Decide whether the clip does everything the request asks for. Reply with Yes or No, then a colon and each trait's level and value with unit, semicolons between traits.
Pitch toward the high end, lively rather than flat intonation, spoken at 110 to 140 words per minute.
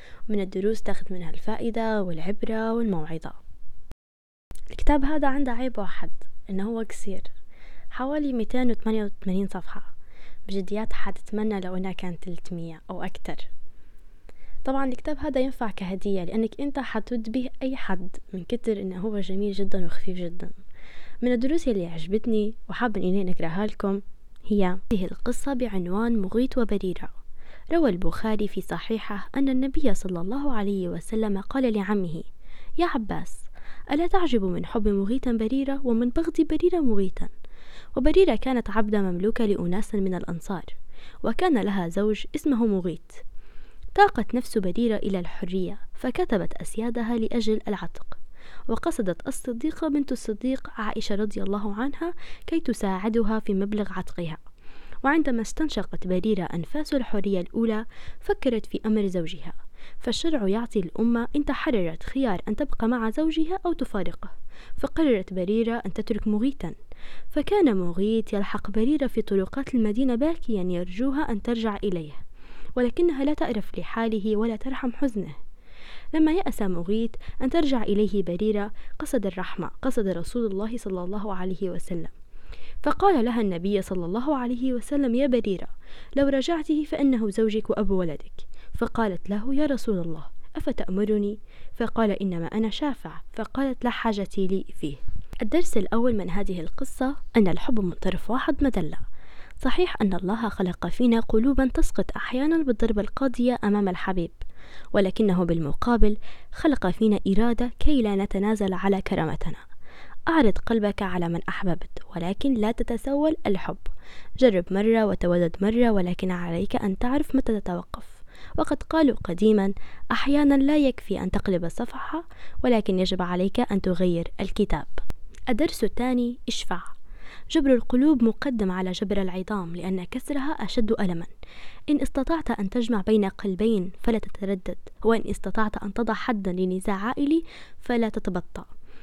No: high, 220 Hz; average, 4.9 semitones; average, 130 wpm